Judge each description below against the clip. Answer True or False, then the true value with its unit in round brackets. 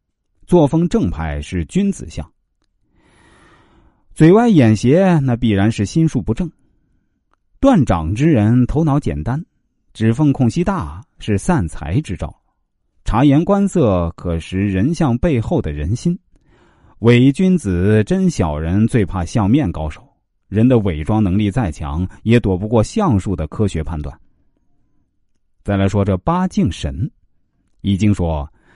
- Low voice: True (110 Hz)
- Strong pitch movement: True (7.7 semitones)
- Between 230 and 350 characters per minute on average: False (190 characters per minute)